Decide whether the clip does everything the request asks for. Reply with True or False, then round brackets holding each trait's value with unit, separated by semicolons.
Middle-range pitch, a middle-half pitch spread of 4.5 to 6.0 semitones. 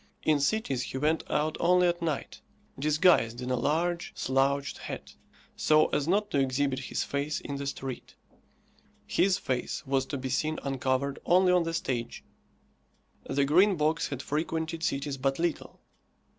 False (145 Hz; 3.5 semitones)